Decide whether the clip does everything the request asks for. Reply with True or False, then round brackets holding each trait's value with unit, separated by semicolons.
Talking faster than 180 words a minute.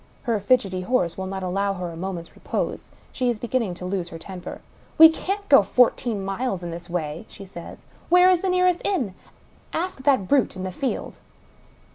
True (200 wpm)